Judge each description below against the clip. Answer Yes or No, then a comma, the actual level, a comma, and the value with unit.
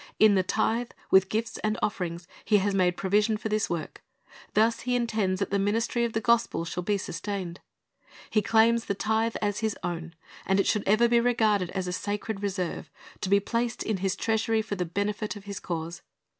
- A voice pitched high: Yes, high, 205 Hz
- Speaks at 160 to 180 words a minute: No, average, 200 wpm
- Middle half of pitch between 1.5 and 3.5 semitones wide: Yes, average, 2.8 semitones